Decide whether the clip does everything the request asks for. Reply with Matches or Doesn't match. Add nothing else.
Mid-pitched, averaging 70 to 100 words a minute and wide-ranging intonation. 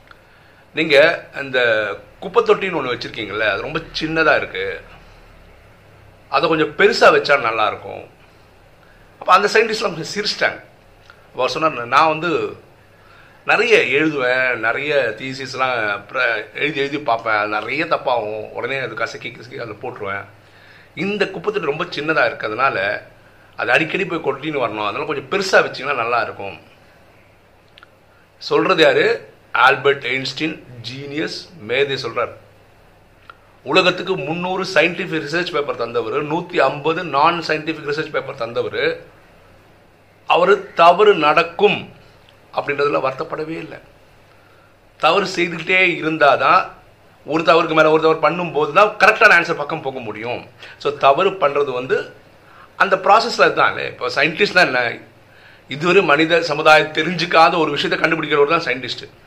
Doesn't match